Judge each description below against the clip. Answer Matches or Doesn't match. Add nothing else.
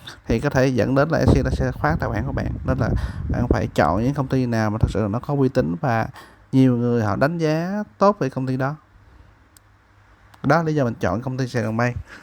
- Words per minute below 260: Matches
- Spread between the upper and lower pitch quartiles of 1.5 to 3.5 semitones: Doesn't match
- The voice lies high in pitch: Doesn't match